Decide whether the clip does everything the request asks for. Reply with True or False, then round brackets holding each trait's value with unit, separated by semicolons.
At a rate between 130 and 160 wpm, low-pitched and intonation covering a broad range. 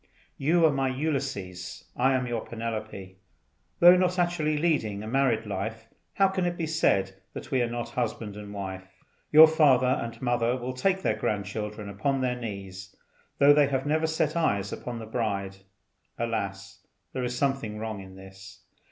False (170 wpm; 120 Hz; 5.8 semitones)